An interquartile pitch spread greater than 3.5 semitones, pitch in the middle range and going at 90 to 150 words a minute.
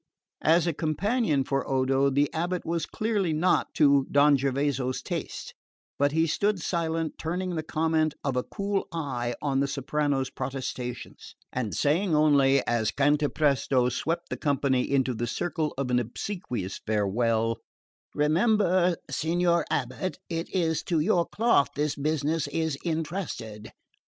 Yes: average, 3.9 semitones; medium, 150 Hz; average, 140 wpm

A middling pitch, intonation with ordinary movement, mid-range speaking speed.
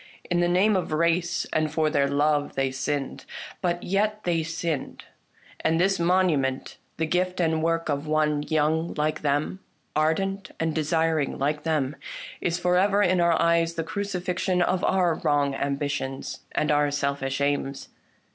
Yes: medium, 160 Hz; average, 3.3 semitones; average, 160 wpm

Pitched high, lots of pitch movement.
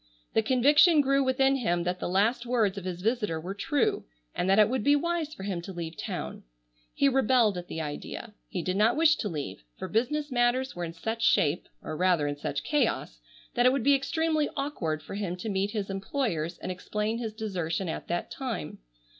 Yes: high, 215 Hz; wide, 6.8 semitones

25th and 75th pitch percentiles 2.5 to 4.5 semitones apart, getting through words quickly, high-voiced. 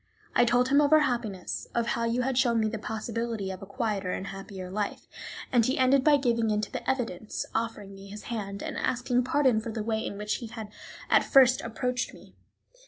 Yes: average, 3.1 semitones; fast, 220 wpm; high, 230 Hz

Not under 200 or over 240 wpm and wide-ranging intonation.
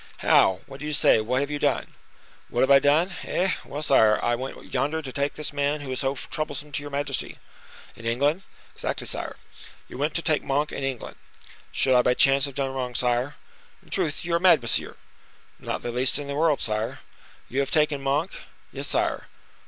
No: fast, 205 wpm; narrow, 2.5 semitones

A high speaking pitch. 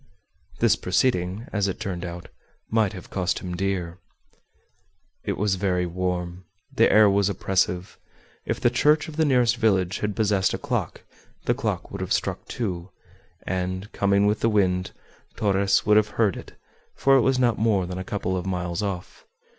No: very low, 95 Hz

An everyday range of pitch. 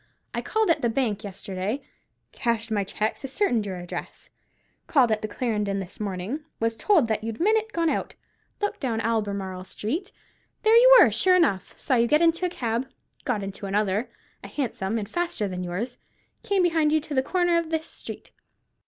No: wide, 8.2 semitones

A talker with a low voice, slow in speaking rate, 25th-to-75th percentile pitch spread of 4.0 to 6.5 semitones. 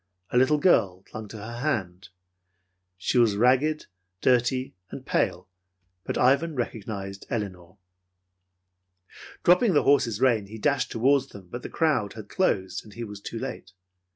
No: low, 115 Hz; average, 155 wpm; average, 4.9 semitones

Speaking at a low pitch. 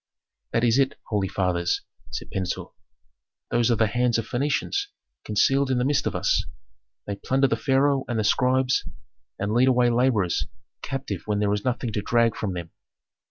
Yes: low, 120 Hz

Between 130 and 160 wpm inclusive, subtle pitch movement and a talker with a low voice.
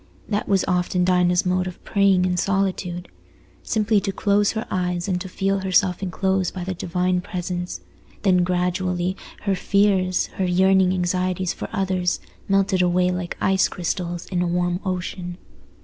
No: average, 155 wpm; narrow, 1.3 semitones; medium, 185 Hz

